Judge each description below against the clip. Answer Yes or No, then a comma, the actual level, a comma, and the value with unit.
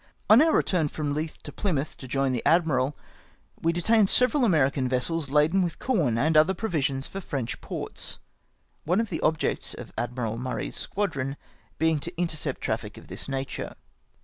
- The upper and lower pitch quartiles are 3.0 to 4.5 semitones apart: No, average, 4.9 semitones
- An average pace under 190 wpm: Yes, average, 170 wpm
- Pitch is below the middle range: No, medium, 155 Hz